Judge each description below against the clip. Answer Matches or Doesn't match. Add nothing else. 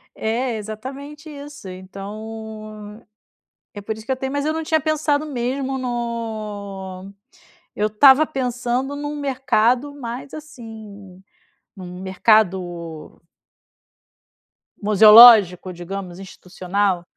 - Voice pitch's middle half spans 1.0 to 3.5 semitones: Doesn't match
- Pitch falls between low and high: Doesn't match